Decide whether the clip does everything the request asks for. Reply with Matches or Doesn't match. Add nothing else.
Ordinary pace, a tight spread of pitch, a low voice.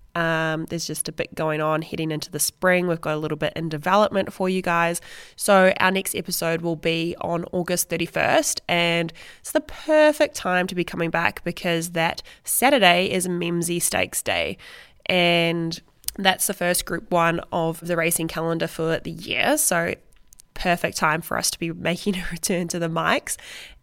Doesn't match